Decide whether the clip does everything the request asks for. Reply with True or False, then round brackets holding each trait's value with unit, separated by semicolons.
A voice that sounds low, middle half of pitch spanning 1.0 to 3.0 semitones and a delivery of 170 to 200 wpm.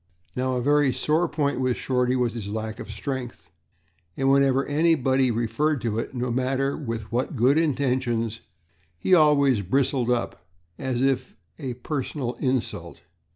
False (130 Hz; 2.5 semitones; 155 wpm)